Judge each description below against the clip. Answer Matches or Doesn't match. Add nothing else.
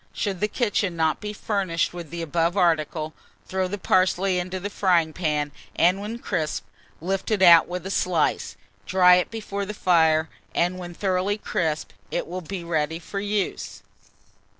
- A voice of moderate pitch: Matches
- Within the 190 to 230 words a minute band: Doesn't match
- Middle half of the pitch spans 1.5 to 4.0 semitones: Matches